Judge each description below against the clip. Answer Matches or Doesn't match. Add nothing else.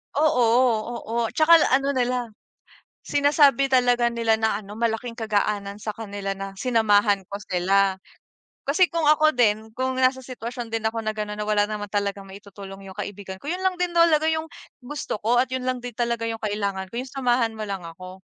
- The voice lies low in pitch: Doesn't match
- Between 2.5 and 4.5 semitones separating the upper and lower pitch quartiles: Matches